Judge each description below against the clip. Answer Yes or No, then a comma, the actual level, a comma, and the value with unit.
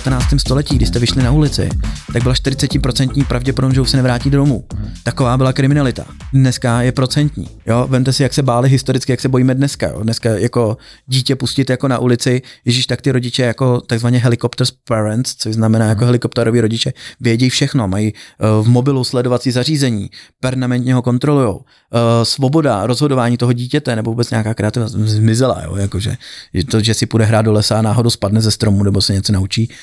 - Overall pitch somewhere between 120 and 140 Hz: Yes, low, 125 Hz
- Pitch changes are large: No, average, 2.8 semitones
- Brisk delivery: Yes, fast, 190 wpm